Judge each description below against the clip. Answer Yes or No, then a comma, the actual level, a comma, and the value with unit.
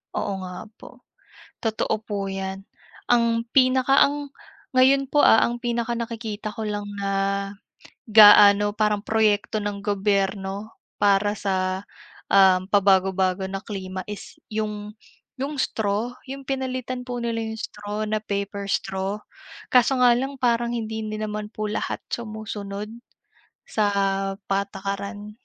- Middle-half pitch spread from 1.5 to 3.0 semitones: Yes, average, 2.7 semitones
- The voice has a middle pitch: No, high, 210 Hz